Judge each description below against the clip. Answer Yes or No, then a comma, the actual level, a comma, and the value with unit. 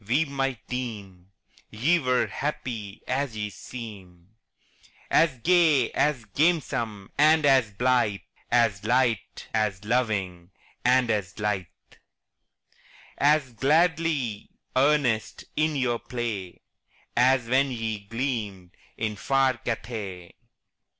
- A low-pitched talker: Yes, low, 120 Hz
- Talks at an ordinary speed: No, slow, 105 wpm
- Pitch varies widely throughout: No, average, 4.5 semitones